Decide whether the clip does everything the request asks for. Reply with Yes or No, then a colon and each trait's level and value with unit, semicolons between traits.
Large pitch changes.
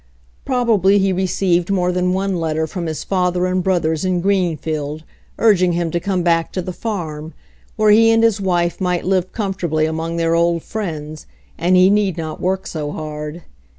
No: average, 2.8 semitones